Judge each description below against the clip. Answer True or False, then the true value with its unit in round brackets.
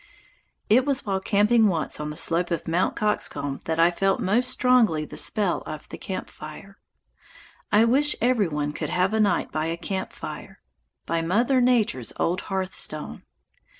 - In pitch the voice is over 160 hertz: True (190 Hz)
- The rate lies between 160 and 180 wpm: True (170 wpm)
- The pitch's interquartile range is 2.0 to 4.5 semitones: False (5.1 semitones)